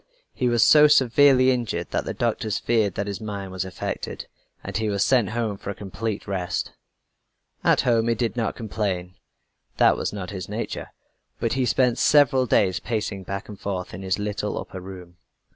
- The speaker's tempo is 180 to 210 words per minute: Yes, average, 185 wpm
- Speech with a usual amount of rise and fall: Yes, average, 3.6 semitones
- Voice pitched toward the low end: Yes, low, 105 Hz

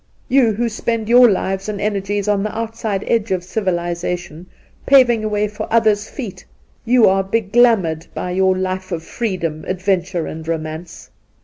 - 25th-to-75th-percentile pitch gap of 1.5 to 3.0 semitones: No, average, 3.8 semitones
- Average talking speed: Yes, average, 170 wpm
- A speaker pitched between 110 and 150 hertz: No, high, 195 Hz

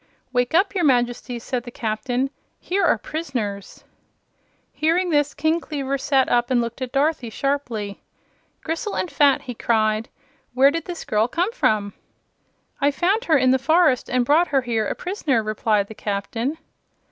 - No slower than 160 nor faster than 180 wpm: Yes, average, 165 wpm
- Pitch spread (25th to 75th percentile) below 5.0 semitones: No, average, 5.3 semitones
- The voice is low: No, very high, 260 Hz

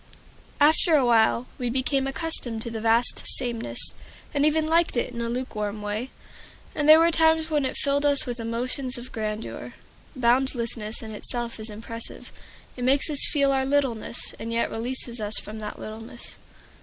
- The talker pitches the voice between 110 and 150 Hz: No, high, 245 Hz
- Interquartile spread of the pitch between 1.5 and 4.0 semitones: Yes, average, 3.7 semitones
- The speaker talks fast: No, average, 170 wpm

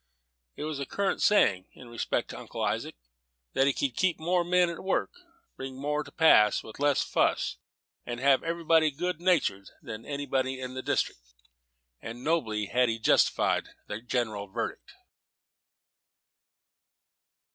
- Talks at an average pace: Yes, average, 150 wpm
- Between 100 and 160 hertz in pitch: Yes, low, 135 Hz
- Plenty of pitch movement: Yes, wide, 5.8 semitones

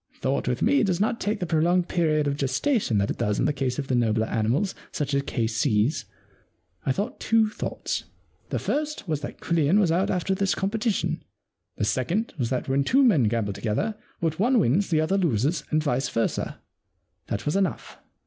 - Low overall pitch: No, medium, 155 Hz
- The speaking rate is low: No, average, 195 wpm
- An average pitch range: No, wide, 7.6 semitones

